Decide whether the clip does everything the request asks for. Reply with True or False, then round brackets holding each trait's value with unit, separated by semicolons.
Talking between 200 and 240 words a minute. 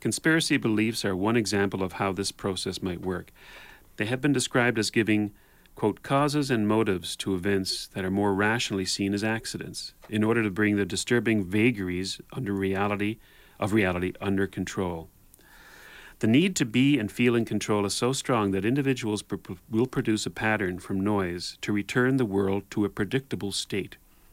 False (175 wpm)